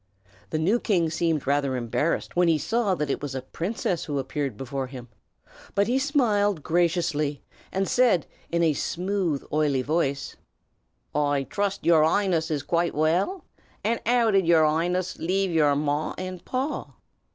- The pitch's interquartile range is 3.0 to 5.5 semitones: Yes, average, 4.9 semitones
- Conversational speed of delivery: Yes, average, 160 wpm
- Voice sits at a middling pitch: Yes, medium, 165 Hz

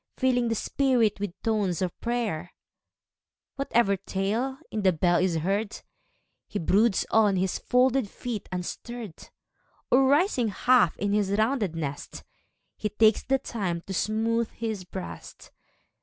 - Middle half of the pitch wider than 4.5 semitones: No, average, 4.0 semitones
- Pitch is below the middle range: No, high, 215 Hz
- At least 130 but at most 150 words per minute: Yes, slow, 135 wpm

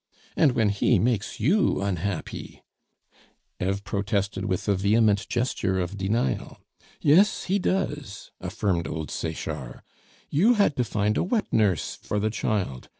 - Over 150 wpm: No, average, 145 wpm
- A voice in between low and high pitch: No, low, 105 Hz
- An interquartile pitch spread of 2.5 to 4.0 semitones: No, average, 4.5 semitones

